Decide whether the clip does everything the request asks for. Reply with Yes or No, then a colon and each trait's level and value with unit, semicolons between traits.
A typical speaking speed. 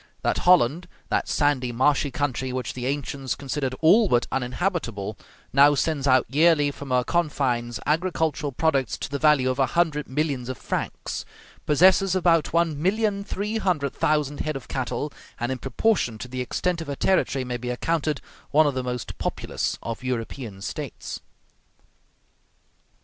Yes: average, 160 wpm